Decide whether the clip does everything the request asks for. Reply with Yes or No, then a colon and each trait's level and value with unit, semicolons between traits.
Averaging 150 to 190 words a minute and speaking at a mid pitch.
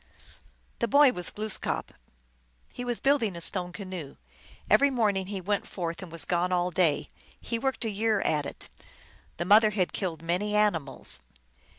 No: average, 165 wpm; high, 195 Hz